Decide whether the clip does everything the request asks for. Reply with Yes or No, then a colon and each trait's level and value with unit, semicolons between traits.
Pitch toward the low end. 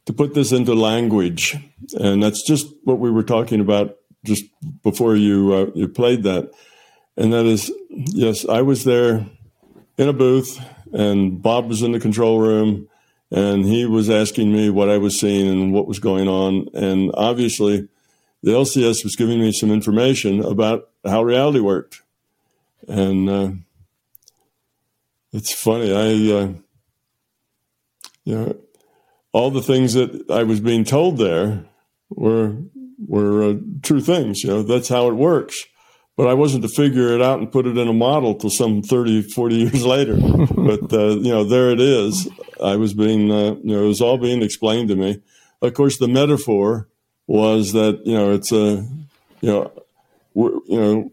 Yes: low, 110 Hz